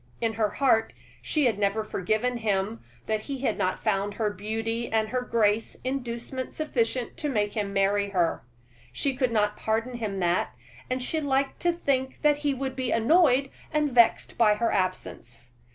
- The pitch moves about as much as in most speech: Yes, average, 4.0 semitones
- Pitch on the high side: Yes, high, 230 Hz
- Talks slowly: No, average, 175 wpm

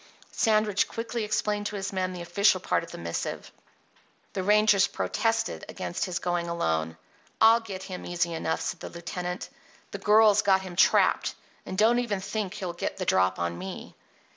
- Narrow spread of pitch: No, average, 3.6 semitones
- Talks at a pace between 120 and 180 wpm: Yes, average, 175 wpm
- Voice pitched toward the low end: No, high, 190 Hz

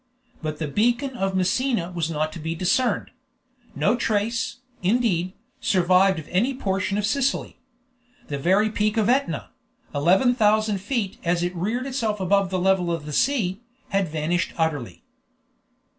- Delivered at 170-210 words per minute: No, average, 150 wpm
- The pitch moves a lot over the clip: No, average, 4.8 semitones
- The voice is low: No, high, 195 Hz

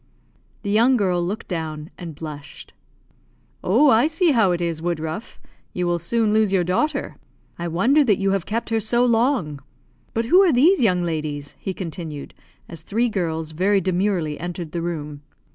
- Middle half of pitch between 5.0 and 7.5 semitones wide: Yes, wide, 5.6 semitones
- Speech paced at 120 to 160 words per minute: No, average, 175 wpm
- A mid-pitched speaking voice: Yes, medium, 180 Hz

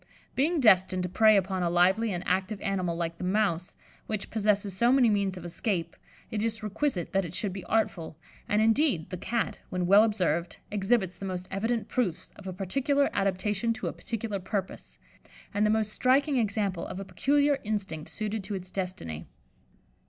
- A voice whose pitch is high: Yes, high, 200 Hz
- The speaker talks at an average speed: Yes, average, 180 wpm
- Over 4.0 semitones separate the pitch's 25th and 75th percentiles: No, average, 3.3 semitones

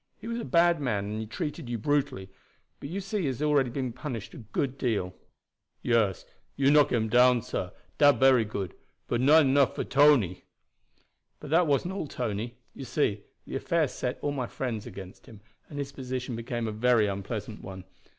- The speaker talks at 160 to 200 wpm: Yes, average, 190 wpm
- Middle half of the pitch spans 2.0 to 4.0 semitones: No, average, 4.7 semitones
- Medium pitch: No, low, 125 Hz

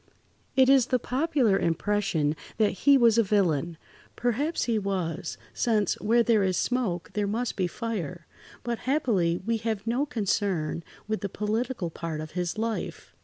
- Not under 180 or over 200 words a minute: No, average, 160 wpm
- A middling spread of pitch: Yes, average, 4.9 semitones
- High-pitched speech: Yes, high, 210 Hz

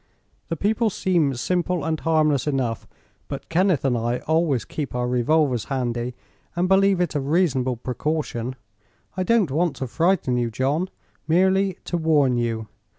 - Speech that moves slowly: No, average, 155 wpm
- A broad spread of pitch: Yes, wide, 5.9 semitones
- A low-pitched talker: No, medium, 150 Hz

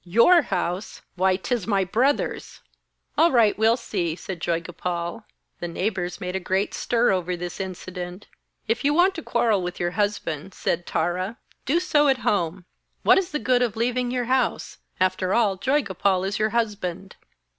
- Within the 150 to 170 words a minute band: Yes, average, 165 wpm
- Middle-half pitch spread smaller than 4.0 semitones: No, average, 4.9 semitones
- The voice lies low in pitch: No, high, 195 Hz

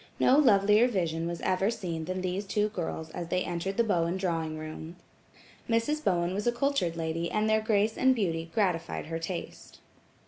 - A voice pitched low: No, medium, 185 Hz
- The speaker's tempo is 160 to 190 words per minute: Yes, average, 180 wpm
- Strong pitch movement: No, average, 4.4 semitones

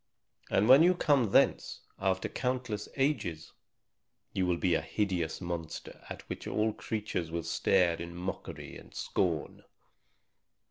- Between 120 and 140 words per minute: Yes, slow, 135 wpm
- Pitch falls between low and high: No, very low, 95 Hz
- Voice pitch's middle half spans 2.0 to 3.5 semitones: No, average, 4.6 semitones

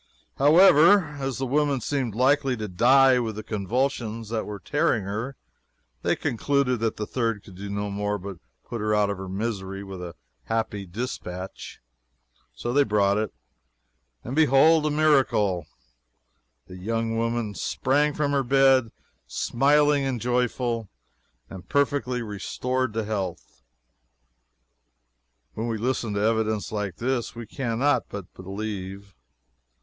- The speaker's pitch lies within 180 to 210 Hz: No, low, 115 Hz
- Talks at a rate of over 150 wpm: No, slow, 135 wpm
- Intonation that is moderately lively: Yes, average, 4.7 semitones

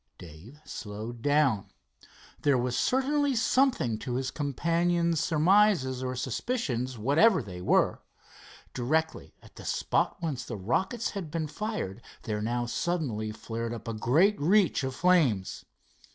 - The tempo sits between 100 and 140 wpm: Yes, slow, 135 wpm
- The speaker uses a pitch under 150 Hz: Yes, medium, 140 Hz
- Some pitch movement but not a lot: No, wide, 7.1 semitones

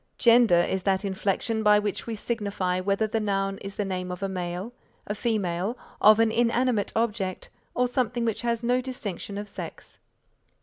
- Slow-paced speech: No, average, 175 wpm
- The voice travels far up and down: No, average, 3.2 semitones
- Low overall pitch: No, high, 210 Hz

